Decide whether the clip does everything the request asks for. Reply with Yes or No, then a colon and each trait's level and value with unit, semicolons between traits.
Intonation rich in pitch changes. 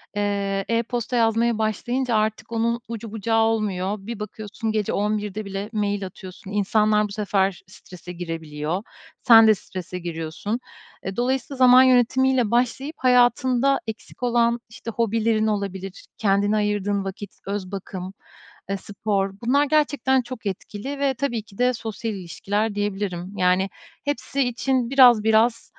No: average, 3.3 semitones